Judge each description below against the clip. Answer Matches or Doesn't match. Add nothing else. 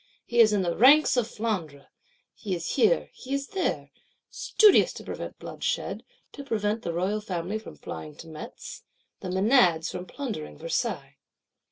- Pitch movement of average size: Doesn't match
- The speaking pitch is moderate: Doesn't match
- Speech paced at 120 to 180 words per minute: Matches